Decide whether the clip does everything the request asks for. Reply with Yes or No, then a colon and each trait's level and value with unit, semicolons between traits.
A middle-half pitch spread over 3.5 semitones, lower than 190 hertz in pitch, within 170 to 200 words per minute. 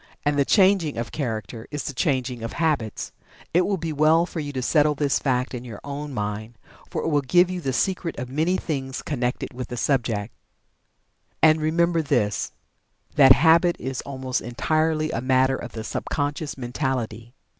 Yes: average, 4.3 semitones; medium, 140 Hz; average, 180 wpm